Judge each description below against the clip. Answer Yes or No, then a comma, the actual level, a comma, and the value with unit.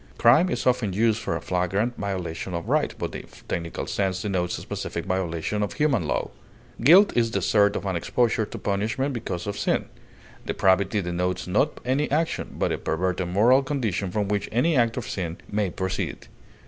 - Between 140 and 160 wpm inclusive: No, average, 180 wpm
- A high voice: No, low, 100 Hz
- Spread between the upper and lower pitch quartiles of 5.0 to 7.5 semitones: No, average, 4.6 semitones